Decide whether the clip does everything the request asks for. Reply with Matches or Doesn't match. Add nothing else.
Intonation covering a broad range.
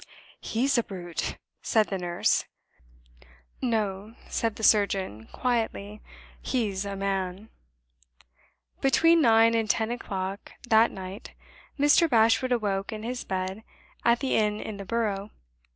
Doesn't match